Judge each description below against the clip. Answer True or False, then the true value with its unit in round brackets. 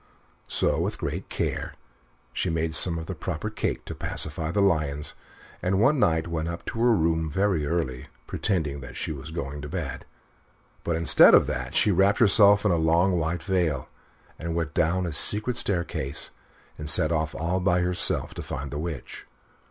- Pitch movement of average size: True (3.1 semitones)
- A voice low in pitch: True (85 Hz)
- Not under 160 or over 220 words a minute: True (185 wpm)